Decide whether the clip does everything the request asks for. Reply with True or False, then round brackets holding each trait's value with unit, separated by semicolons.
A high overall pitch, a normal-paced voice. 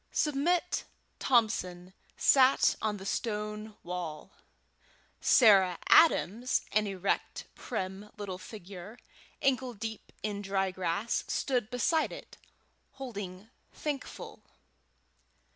False (210 Hz; 95 wpm)